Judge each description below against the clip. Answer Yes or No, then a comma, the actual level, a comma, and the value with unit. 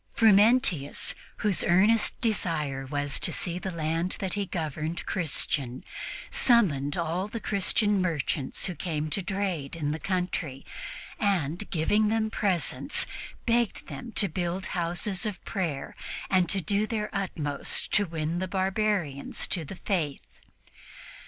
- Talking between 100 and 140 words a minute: Yes, slow, 135 wpm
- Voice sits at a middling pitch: Yes, medium, 180 Hz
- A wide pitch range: No, average, 4.6 semitones